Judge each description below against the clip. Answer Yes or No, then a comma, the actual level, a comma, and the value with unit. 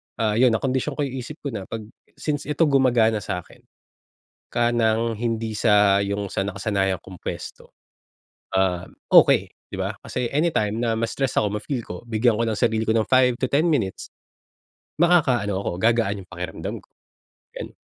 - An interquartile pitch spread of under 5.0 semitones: Yes, average, 3.9 semitones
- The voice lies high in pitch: No, low, 115 Hz